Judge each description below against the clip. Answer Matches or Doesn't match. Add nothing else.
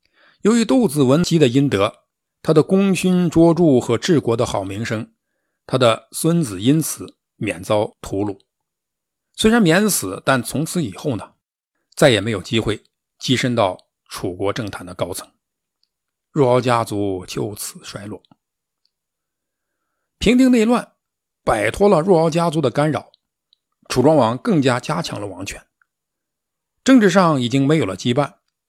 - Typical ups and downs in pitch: Doesn't match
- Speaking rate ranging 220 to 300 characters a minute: Doesn't match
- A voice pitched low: Doesn't match